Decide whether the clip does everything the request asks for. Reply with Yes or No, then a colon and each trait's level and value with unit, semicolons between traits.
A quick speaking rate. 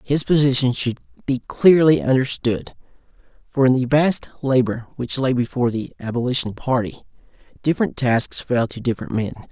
No: average, 145 wpm